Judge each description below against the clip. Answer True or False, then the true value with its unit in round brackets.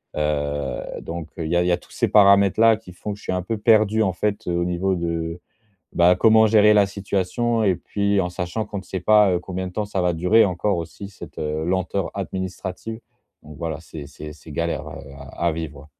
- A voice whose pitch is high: False (90 Hz)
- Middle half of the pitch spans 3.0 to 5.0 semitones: True (3.5 semitones)